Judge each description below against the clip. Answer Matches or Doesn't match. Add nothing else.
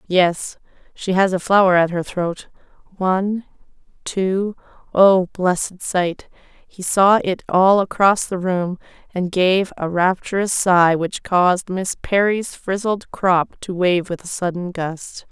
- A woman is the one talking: Matches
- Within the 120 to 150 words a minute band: Matches